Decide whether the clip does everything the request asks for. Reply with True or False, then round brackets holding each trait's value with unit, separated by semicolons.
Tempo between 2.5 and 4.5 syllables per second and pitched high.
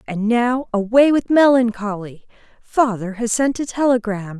True (4.4 syllables/s; 230 Hz)